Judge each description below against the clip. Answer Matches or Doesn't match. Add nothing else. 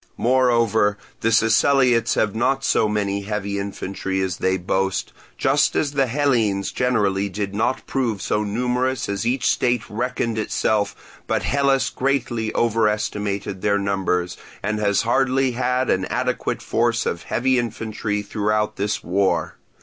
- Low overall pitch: Matches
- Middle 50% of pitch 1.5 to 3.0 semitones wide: Doesn't match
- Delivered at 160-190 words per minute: Doesn't match